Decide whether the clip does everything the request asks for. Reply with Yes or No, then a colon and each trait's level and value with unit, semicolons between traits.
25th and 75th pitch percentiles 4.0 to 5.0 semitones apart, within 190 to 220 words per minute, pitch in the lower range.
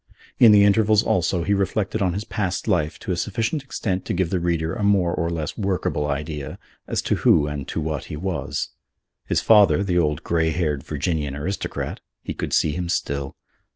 Yes: average, 4.5 semitones; average, 195 wpm; very low, 85 Hz